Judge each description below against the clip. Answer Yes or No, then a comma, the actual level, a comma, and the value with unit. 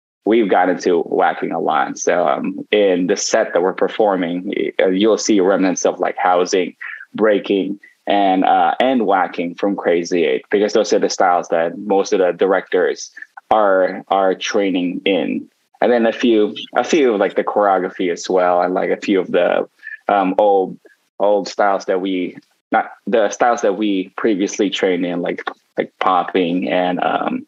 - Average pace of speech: Yes, average, 175 wpm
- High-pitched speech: Yes, very high, 270 Hz